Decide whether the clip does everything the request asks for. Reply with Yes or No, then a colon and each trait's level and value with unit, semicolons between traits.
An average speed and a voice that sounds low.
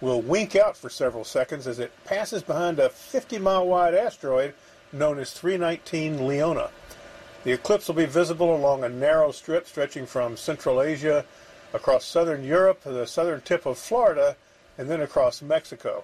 No: average, 170 wpm; medium, 170 Hz